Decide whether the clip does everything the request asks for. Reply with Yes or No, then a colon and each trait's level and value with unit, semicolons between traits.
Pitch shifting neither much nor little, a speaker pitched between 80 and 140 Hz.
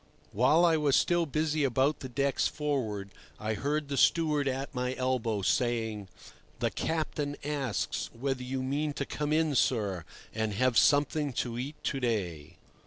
Yes: average, 4.2 semitones; low, 135 Hz